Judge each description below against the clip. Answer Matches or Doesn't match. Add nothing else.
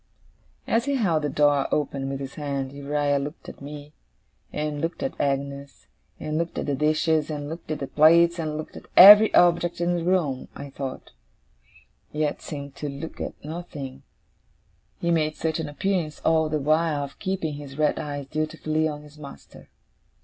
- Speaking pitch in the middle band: Matches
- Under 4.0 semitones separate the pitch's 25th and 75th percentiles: Matches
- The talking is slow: Doesn't match